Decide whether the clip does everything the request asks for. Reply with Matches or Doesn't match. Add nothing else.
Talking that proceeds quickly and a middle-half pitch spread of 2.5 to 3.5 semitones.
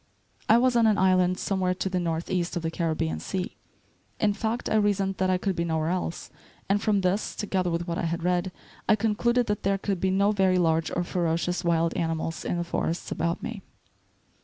Matches